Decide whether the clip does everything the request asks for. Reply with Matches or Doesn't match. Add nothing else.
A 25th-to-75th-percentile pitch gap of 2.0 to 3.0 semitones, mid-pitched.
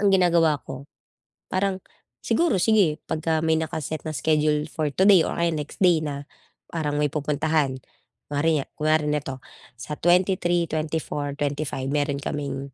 Matches